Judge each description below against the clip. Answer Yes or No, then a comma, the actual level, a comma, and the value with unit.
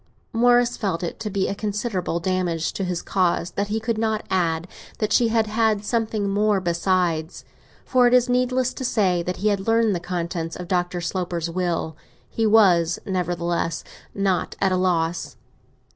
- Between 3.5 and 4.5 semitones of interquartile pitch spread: Yes, average, 4.0 semitones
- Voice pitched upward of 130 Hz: Yes, high, 190 Hz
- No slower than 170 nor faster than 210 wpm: Yes, average, 175 wpm